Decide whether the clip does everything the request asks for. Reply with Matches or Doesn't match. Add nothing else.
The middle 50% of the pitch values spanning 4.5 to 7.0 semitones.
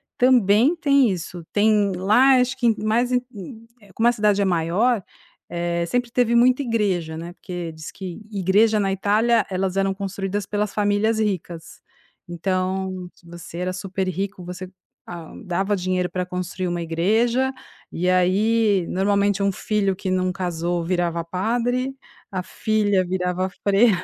Doesn't match